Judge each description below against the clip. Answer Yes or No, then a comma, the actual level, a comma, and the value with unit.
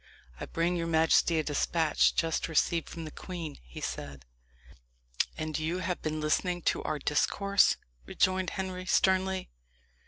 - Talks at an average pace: Yes, average, 145 wpm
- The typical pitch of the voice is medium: Yes, medium, 165 Hz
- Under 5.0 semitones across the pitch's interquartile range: Yes, average, 2.9 semitones